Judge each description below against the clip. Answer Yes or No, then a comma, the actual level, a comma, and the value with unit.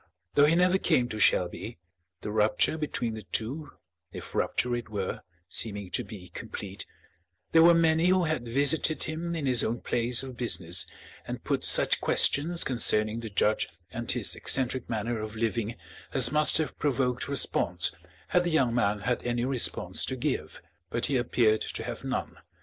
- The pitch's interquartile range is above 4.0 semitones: Yes, wide, 5.4 semitones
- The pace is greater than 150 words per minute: Yes, average, 170 wpm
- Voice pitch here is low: Yes, low, 120 Hz